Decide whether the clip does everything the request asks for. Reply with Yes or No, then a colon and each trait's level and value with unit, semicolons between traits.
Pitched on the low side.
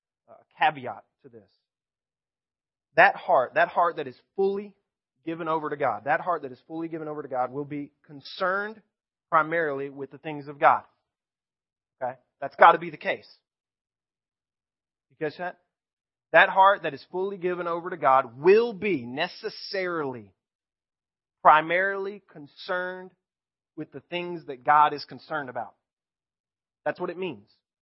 No: medium, 155 Hz